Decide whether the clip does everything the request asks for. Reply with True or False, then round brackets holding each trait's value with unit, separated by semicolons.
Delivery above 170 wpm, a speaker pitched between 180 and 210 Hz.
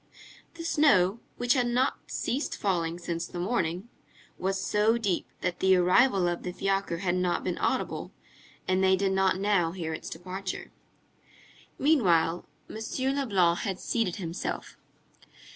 False (145 wpm; 190 Hz)